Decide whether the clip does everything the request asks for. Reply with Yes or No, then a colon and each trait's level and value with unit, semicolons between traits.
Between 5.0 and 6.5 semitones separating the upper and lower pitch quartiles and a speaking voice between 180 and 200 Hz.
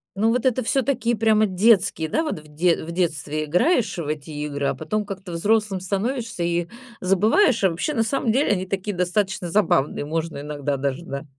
Yes: wide, 5.6 semitones; medium, 185 Hz